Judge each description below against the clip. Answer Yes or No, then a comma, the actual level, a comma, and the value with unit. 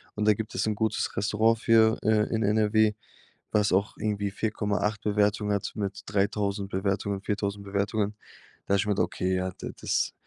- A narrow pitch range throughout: Yes, narrow, 1.3 semitones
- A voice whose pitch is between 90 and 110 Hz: Yes, low, 105 Hz